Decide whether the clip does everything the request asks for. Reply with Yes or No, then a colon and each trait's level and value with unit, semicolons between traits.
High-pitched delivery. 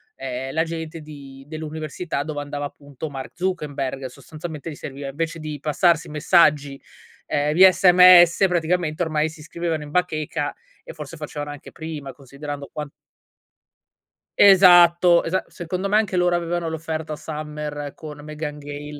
No: medium, 155 Hz